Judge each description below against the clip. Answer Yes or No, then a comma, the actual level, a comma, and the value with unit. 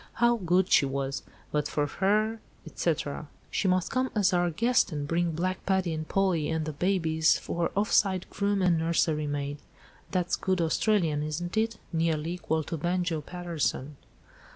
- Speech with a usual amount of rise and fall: Yes, average, 3.4 semitones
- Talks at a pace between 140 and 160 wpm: Yes, average, 155 wpm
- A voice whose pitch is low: No, medium, 175 Hz